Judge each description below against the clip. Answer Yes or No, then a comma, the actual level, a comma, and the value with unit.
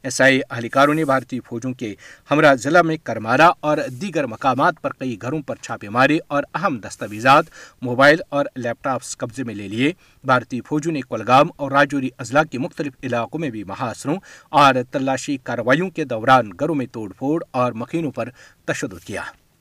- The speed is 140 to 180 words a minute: Yes, average, 175 wpm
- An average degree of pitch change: Yes, average, 3.5 semitones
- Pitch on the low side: Yes, low, 130 Hz